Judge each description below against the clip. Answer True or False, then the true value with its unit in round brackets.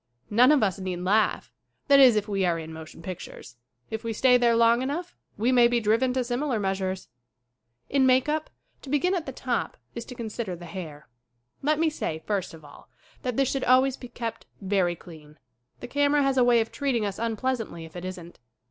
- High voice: True (230 Hz)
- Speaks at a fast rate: True (210 wpm)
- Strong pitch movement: True (5.7 semitones)